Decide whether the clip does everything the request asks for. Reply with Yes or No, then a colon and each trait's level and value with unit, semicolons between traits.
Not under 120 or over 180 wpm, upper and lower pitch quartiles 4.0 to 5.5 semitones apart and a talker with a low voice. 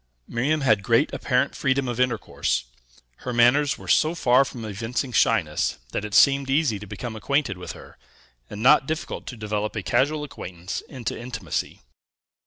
Yes: average, 165 wpm; average, 4.4 semitones; low, 125 Hz